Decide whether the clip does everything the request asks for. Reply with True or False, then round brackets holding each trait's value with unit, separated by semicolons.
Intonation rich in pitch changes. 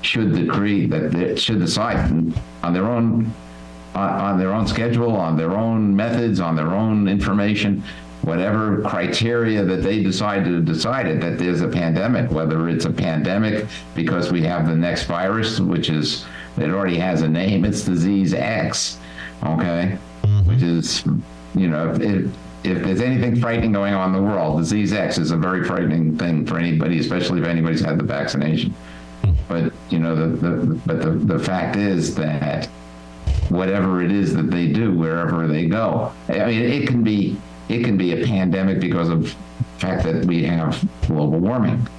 False (4.2 semitones)